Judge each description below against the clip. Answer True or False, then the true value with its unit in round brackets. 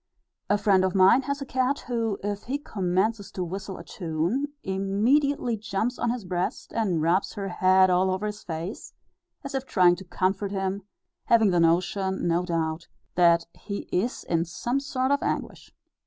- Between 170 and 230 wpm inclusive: True (175 wpm)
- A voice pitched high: True (195 Hz)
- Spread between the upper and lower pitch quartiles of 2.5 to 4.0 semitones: False (4.4 semitones)